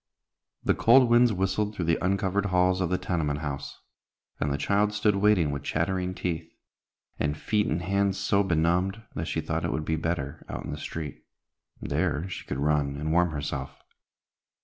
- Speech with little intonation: No, average, 4.3 semitones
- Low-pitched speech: Yes, very low, 90 Hz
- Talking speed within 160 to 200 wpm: Yes, average, 180 wpm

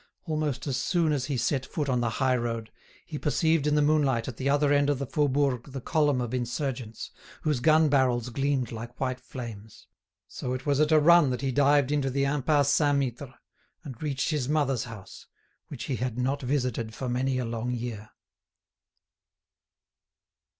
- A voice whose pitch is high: No, low, 135 Hz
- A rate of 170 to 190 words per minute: Yes, average, 185 wpm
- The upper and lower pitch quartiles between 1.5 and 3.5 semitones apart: Yes, average, 2.9 semitones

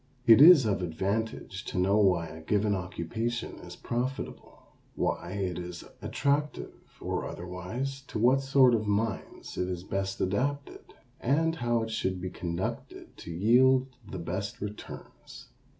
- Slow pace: No, average, 145 wpm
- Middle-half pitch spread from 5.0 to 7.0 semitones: Yes, wide, 5.6 semitones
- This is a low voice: Yes, low, 105 Hz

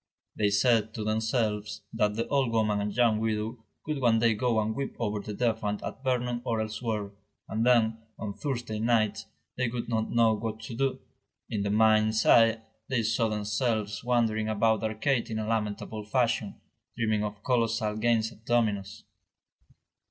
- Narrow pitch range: Yes, narrow, 1.6 semitones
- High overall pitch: No, low, 110 Hz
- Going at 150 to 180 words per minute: Yes, average, 170 wpm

